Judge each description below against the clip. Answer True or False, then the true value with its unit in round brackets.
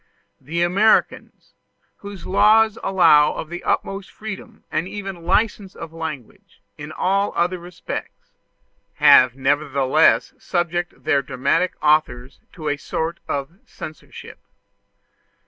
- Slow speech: True (110 wpm)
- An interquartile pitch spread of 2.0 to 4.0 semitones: False (4.4 semitones)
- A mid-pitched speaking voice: True (170 Hz)